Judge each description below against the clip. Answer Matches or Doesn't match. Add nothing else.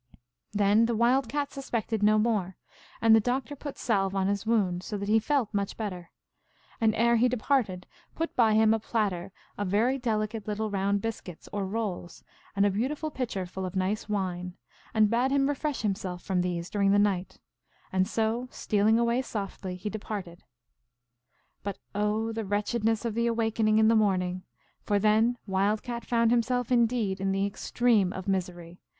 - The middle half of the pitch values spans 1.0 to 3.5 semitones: Matches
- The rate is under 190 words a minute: Matches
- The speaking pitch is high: Matches